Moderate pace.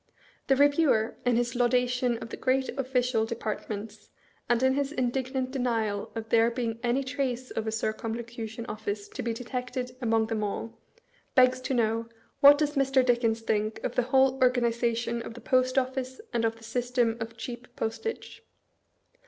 Yes: average, 170 wpm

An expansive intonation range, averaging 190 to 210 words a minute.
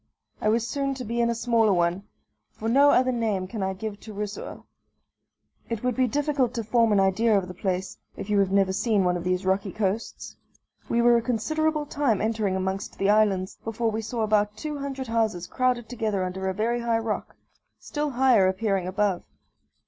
No: average, 3.6 semitones; average, 200 wpm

